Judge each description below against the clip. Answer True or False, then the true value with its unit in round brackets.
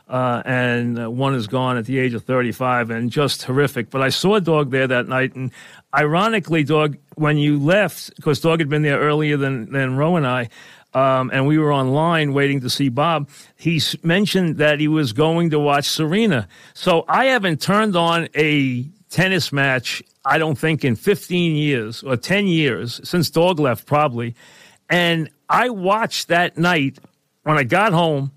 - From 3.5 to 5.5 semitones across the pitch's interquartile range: True (4.2 semitones)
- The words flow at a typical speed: True (180 wpm)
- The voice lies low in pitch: False (150 Hz)